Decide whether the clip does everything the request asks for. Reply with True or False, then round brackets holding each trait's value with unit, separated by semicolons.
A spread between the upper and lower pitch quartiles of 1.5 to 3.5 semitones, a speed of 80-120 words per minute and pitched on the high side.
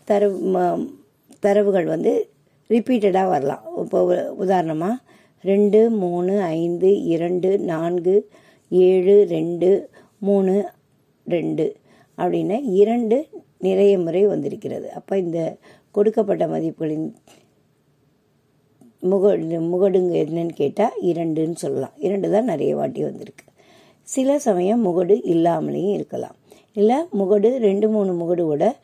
True (3.0 semitones; 95 wpm; 195 Hz)